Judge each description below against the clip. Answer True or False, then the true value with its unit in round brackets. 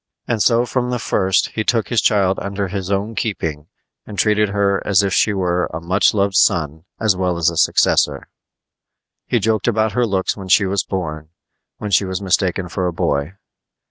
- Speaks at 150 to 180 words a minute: False (195 wpm)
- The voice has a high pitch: False (95 Hz)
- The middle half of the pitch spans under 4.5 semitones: True (2.9 semitones)